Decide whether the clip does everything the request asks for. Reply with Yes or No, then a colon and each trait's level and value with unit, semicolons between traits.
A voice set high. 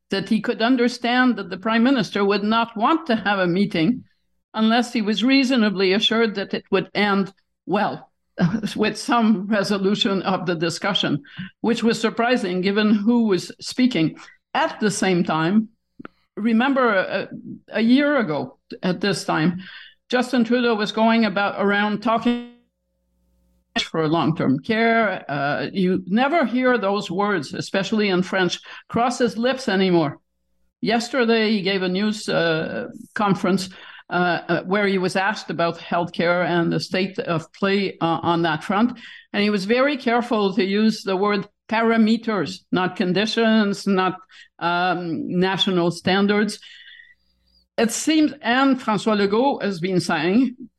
Yes: high, 205 Hz